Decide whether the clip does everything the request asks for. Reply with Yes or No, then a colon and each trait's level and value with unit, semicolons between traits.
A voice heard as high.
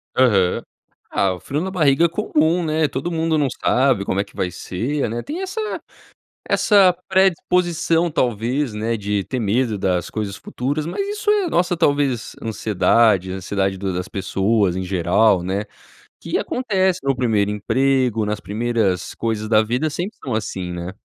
No: low, 120 Hz